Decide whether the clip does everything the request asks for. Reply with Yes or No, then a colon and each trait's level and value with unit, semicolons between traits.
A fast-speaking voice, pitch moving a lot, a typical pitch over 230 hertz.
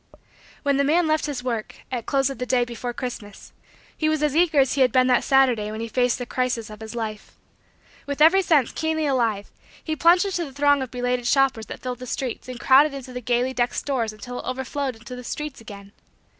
No: fast, 225 wpm; average, 3.0 semitones; very high, 255 Hz